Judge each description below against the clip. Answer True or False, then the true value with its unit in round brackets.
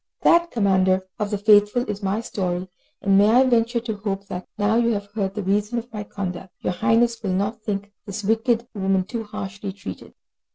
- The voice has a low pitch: False (205 Hz)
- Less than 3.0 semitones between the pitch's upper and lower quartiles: True (2.5 semitones)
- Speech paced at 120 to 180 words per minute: False (200 wpm)